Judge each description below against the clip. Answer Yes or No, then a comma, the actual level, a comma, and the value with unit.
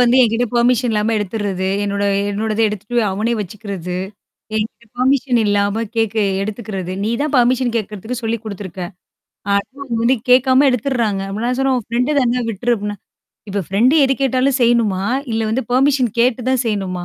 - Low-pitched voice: No, high, 230 Hz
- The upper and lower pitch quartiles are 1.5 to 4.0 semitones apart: Yes, average, 3.5 semitones